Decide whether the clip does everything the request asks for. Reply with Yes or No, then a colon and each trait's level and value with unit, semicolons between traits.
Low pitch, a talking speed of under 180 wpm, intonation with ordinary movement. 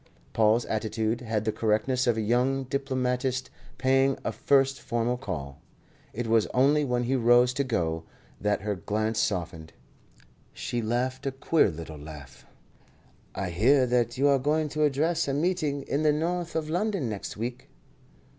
Yes: low, 125 Hz; average, 160 wpm; average, 4.2 semitones